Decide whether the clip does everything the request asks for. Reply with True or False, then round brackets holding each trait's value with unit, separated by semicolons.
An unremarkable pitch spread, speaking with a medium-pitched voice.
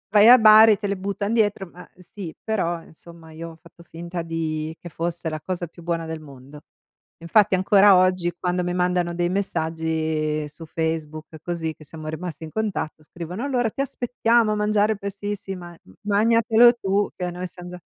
True (4.1 semitones; 180 Hz)